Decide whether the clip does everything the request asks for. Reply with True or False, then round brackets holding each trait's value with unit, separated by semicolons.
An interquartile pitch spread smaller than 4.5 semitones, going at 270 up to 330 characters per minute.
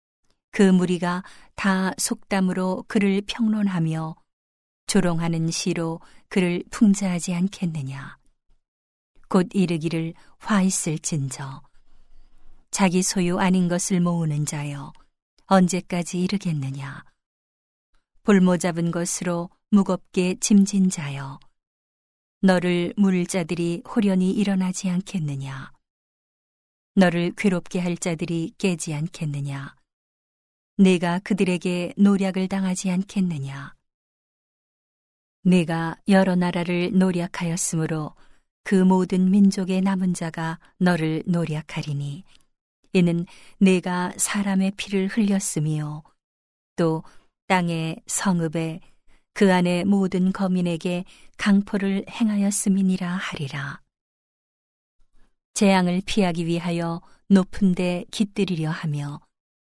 False (2.6 semitones; 215 characters per minute)